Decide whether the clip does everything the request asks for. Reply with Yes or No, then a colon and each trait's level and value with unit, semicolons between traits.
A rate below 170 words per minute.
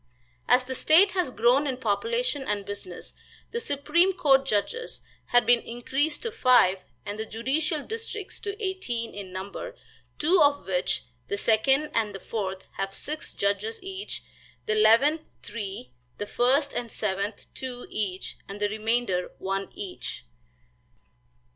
Yes: average, 145 wpm